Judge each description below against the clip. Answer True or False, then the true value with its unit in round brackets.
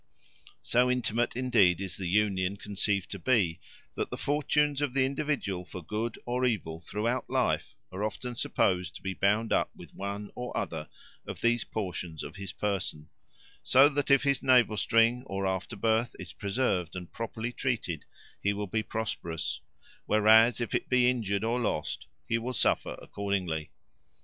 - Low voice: True (105 Hz)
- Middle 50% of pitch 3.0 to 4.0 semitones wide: False (4.5 semitones)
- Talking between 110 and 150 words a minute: False (165 wpm)